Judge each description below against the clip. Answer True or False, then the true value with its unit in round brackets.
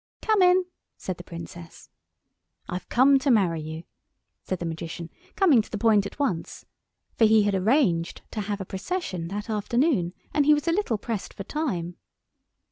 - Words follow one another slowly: False (175 wpm)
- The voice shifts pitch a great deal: True (7.9 semitones)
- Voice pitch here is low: False (210 Hz)